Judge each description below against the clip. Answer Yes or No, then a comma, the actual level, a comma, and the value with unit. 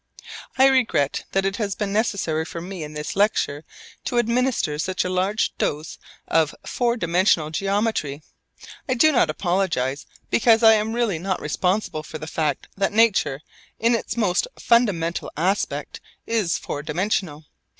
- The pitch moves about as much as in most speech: No, wide, 5.9 semitones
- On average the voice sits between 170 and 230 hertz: Yes, high, 190 Hz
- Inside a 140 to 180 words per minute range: Yes, average, 150 wpm